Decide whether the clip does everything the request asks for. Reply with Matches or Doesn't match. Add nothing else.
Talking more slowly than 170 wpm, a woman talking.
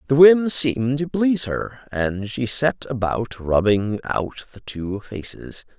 Doesn't match